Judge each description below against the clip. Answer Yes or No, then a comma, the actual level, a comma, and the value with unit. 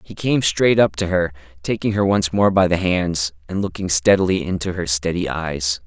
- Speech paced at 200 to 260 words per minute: Yes, fast, 205 wpm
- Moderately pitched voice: No, very low, 90 Hz